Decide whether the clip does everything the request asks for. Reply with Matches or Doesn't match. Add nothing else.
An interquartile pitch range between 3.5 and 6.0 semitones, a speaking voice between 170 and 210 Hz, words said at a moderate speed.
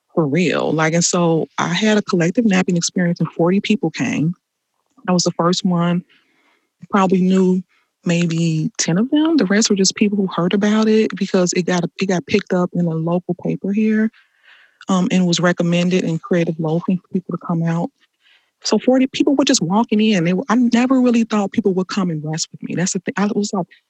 Doesn't match